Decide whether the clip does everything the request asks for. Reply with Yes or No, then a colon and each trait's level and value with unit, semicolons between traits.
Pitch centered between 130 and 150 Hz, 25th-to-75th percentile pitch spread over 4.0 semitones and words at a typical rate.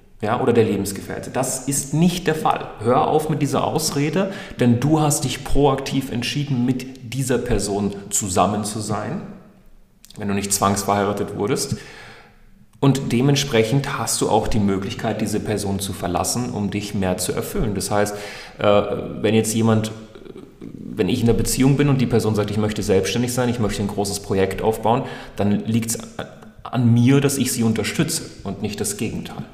No: low, 115 Hz; average, 4.6 semitones; average, 175 wpm